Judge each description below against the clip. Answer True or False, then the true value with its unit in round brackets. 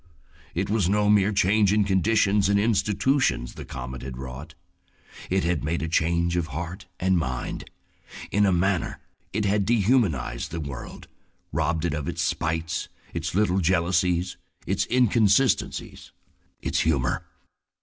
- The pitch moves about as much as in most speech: True (4.1 semitones)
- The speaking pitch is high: False (90 Hz)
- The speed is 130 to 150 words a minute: True (145 wpm)